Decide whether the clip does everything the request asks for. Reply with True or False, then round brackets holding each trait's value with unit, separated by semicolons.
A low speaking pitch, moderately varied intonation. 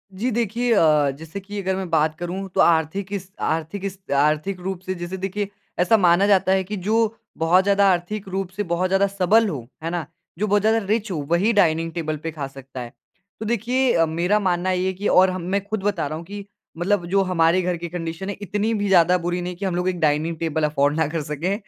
False (185 Hz; 3.3 semitones)